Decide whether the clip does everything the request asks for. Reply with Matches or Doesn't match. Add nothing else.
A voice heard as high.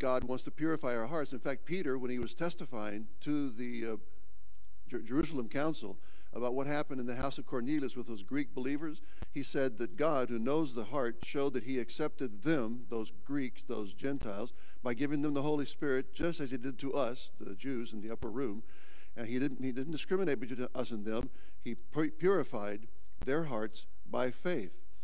Doesn't match